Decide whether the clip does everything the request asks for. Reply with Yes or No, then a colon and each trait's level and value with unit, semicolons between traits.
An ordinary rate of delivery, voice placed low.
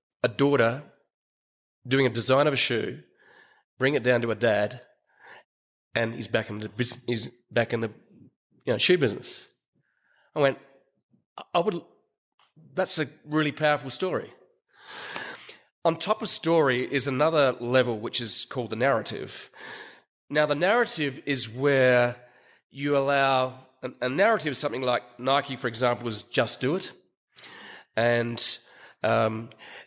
Yes: average, 145 wpm; low, 130 Hz